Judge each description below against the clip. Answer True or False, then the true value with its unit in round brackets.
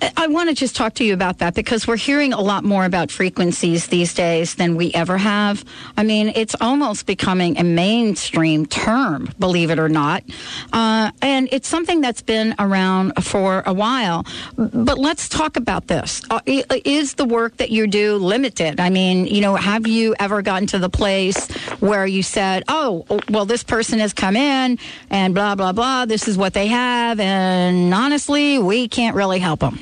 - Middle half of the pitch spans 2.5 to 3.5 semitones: False (4.4 semitones)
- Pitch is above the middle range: True (210 Hz)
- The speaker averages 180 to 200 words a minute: True (190 wpm)